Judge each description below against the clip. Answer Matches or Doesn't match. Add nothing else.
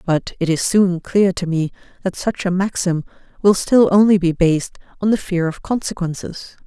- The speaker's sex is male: Doesn't match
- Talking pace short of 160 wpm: Doesn't match